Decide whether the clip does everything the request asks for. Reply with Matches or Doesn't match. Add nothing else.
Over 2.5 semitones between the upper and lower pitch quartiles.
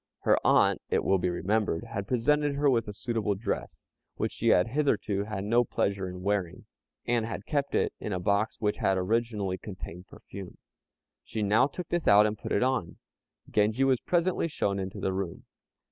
Matches